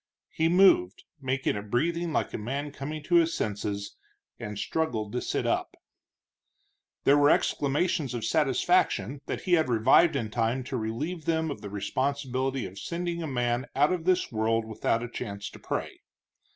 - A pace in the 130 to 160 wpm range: No, average, 170 wpm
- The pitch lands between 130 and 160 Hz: Yes, low, 135 Hz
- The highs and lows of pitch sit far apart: Yes, wide, 6.1 semitones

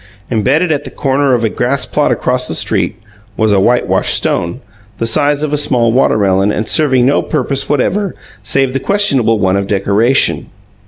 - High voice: No, low, 130 Hz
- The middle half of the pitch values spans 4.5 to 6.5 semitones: Yes, average, 4.8 semitones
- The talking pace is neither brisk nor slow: Yes, average, 170 wpm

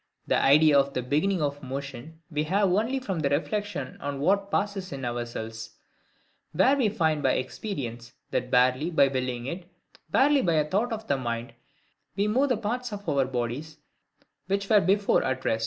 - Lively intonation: Yes, wide, 7.4 semitones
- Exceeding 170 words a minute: Yes, average, 180 wpm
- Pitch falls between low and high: Yes, medium, 155 Hz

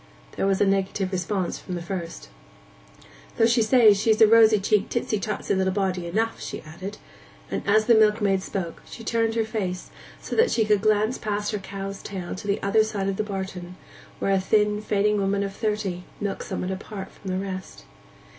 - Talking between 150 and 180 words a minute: No, average, 195 wpm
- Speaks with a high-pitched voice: Yes, high, 200 Hz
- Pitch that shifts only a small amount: Yes, narrow, 2.1 semitones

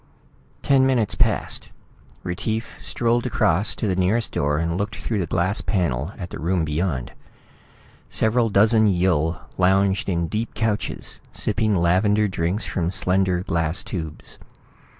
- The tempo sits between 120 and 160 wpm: Yes, slow, 135 wpm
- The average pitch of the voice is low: Yes, very low, 95 Hz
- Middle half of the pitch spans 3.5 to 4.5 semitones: Yes, average, 4.1 semitones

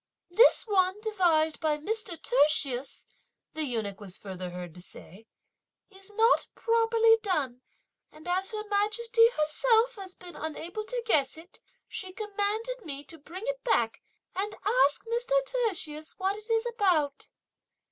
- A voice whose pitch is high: Yes, very high, 375 Hz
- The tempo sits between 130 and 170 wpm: Yes, average, 145 wpm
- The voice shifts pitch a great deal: Yes, wide, 6.9 semitones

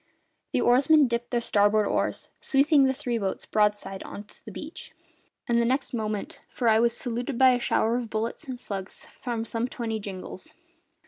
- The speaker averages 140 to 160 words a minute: No, average, 180 wpm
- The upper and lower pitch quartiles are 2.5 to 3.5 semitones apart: Yes, average, 2.9 semitones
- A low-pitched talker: No, high, 235 Hz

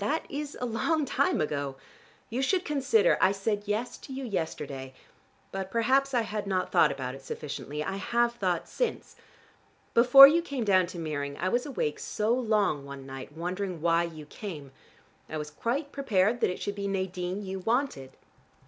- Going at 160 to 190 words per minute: Yes, average, 180 wpm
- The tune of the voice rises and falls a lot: Yes, wide, 7.6 semitones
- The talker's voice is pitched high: Yes, high, 195 Hz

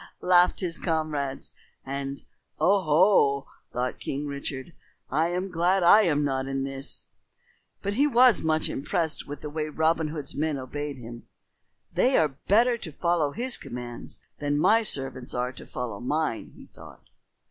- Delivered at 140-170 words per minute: Yes, average, 160 wpm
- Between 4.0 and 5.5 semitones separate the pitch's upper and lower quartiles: Yes, average, 4.5 semitones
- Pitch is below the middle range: No, medium, 150 Hz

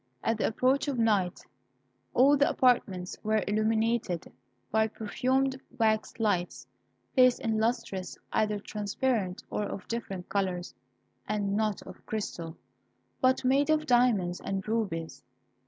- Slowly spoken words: Yes, slow, 125 wpm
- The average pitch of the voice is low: No, high, 220 Hz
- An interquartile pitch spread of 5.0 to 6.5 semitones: No, average, 4.1 semitones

